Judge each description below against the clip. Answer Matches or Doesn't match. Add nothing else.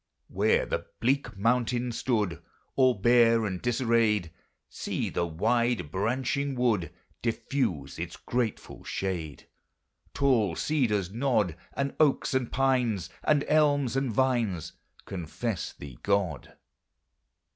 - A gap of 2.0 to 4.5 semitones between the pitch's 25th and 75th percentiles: Doesn't match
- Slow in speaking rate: Matches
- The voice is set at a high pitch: Doesn't match